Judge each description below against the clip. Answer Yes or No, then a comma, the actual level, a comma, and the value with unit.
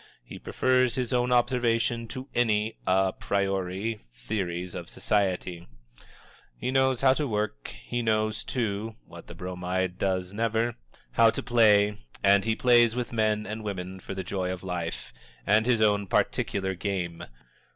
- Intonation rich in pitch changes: No, average, 3.8 semitones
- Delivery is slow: No, average, 155 wpm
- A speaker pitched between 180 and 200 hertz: No, low, 105 Hz